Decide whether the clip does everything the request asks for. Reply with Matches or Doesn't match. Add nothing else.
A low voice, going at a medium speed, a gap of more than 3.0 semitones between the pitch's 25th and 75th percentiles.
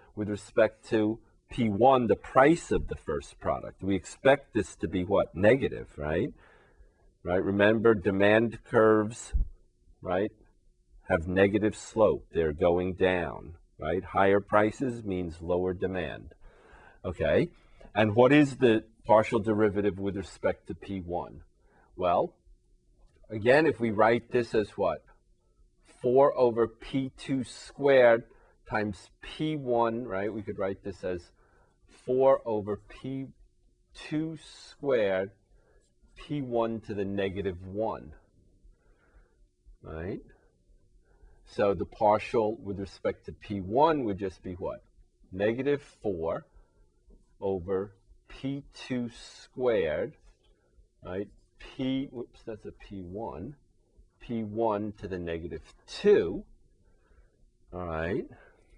Doesn't match